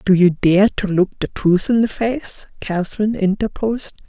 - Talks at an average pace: Yes, average, 175 wpm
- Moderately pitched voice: No, high, 200 Hz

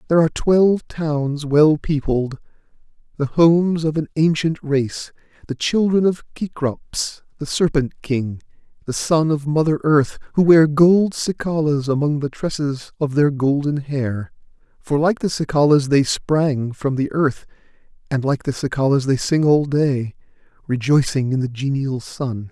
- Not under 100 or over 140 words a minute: No, average, 150 wpm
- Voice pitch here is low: No, medium, 145 Hz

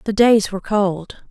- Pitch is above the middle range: Yes, high, 205 Hz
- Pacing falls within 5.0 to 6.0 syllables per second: No, 4.4 syllables/s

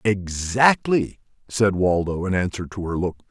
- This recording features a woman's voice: No, male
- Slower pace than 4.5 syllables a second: Yes, 4.3 syllables/s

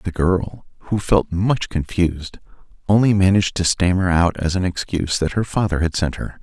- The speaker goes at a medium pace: Yes, average, 185 wpm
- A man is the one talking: Yes, male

